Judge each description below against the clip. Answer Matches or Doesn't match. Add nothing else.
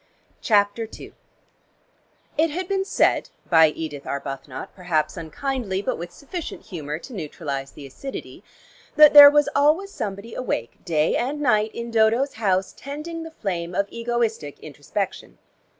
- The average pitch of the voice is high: Matches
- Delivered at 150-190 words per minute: Doesn't match